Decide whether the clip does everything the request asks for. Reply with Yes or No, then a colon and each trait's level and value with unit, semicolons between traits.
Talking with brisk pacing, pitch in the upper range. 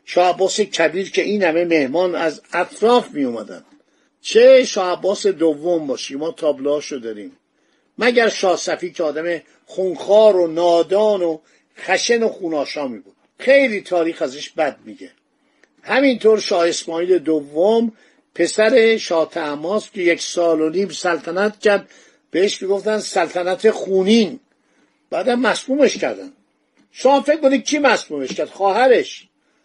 No: average, 130 wpm; high, 195 Hz